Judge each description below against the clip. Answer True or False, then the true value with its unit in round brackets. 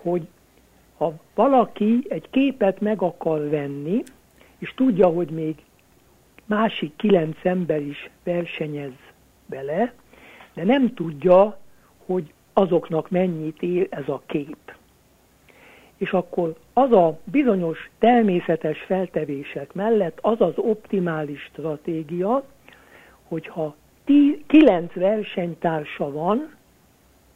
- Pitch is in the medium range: True (180 Hz)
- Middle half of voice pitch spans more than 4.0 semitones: True (5.1 semitones)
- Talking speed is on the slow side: True (100 wpm)